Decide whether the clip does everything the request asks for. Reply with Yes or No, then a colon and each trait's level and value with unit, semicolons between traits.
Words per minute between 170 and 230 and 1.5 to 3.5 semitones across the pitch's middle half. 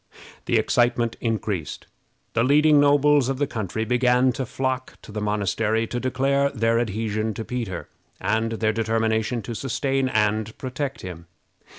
No: average, 150 wpm; average, 3.1 semitones